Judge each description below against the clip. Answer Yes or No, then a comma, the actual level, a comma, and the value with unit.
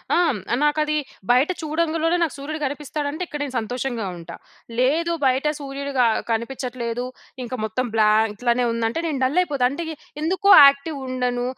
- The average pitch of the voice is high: Yes, very high, 275 Hz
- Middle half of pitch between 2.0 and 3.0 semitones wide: No, average, 3.8 semitones